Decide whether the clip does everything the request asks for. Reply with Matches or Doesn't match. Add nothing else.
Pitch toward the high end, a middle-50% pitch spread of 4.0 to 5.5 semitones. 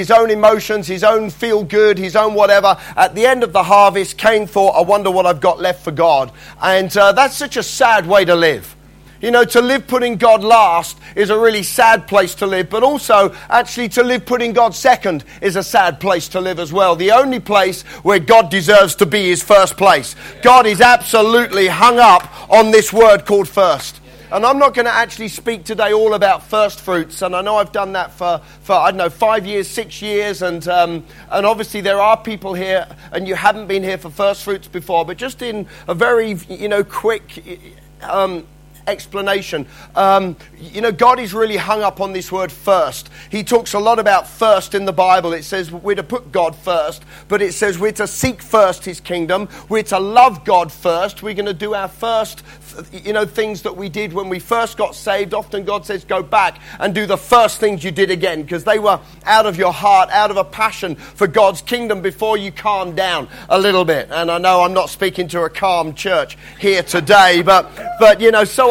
Doesn't match